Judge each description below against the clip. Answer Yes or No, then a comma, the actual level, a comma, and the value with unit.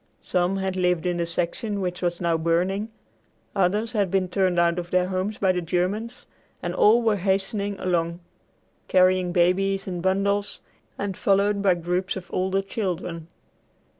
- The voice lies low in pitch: No, medium, 185 Hz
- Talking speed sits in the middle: Yes, average, 160 wpm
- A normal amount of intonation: No, narrow, 2.0 semitones